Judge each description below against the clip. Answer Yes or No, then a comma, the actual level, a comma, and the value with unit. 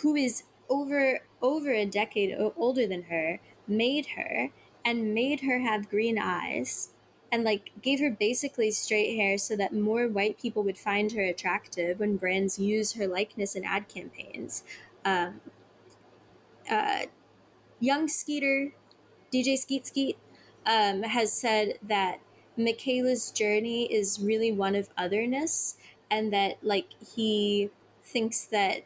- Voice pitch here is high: Yes, high, 215 Hz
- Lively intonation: No, average, 3.8 semitones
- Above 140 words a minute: No, slow, 135 wpm